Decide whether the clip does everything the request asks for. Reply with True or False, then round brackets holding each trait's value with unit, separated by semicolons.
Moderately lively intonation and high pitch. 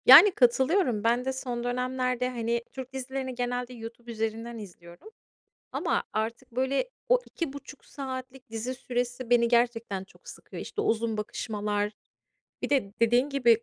False (2.3 semitones; 245 Hz)